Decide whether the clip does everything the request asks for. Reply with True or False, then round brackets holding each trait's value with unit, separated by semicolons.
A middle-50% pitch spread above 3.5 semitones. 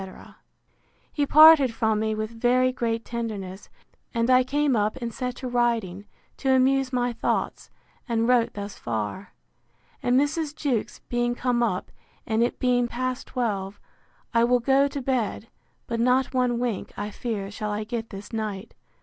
False (2.8 semitones)